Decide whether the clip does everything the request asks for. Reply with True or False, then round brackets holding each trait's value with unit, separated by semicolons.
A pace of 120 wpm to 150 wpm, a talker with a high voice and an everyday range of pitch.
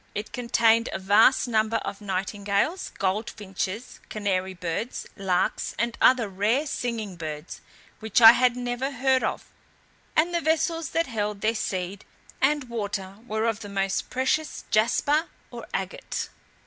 True (145 wpm; 220 Hz; 4.0 semitones)